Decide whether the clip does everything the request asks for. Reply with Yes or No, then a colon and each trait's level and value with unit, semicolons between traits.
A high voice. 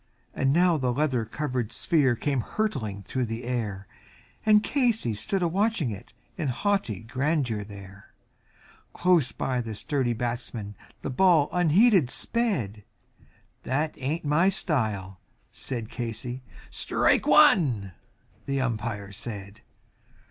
No: low, 125 Hz